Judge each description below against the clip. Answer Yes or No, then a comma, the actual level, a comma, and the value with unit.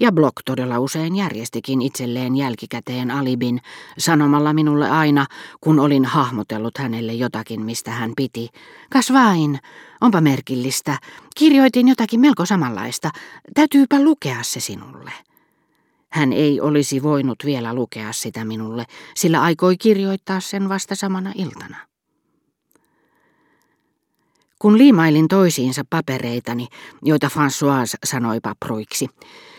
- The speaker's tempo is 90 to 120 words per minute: Yes, average, 105 wpm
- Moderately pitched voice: Yes, medium, 145 Hz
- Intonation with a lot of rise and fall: Yes, wide, 7.3 semitones